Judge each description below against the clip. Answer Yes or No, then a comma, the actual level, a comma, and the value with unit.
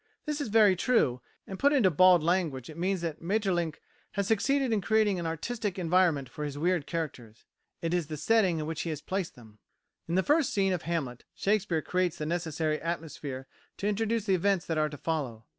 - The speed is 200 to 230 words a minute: Yes, fast, 205 wpm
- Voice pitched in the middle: Yes, medium, 175 Hz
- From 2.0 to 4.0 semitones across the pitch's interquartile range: No, average, 4.5 semitones